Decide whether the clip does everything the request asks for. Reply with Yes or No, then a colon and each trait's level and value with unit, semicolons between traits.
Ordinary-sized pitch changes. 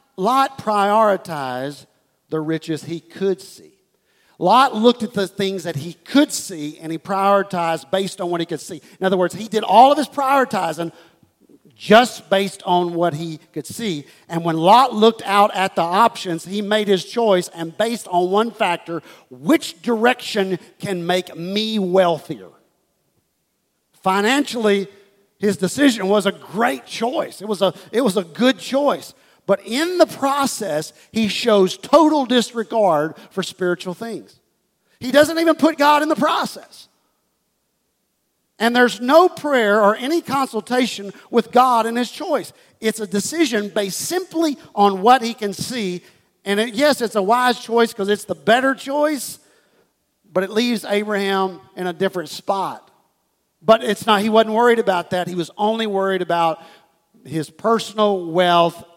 Yes: average, 4.8 semitones